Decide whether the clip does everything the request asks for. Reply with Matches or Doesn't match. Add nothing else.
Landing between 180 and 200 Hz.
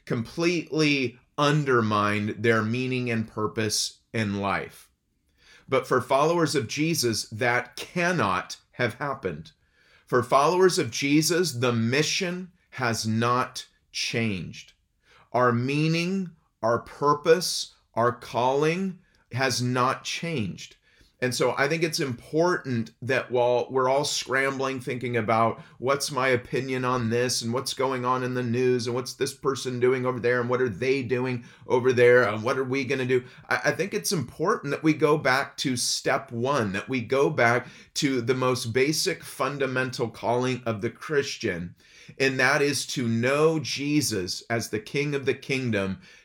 Doesn't match